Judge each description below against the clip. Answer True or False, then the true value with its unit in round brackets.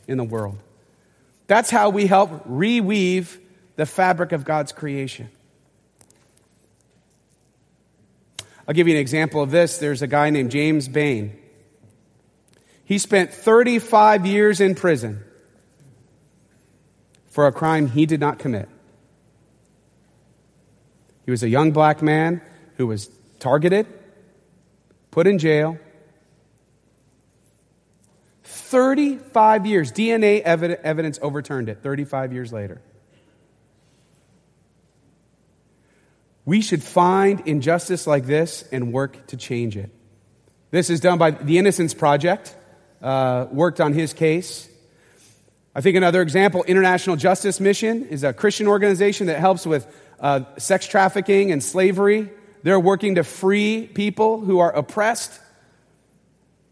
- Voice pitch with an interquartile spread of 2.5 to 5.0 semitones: False (5.6 semitones)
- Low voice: False (165 Hz)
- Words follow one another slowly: True (115 wpm)